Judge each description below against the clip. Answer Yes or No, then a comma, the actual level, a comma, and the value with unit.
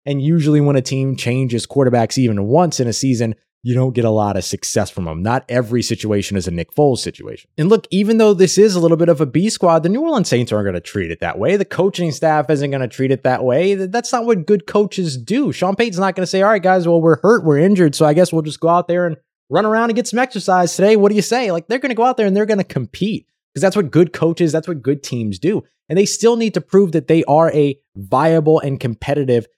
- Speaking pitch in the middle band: Yes, medium, 160 Hz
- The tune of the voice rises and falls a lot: Yes, wide, 7.1 semitones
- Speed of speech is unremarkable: No, fast, 280 wpm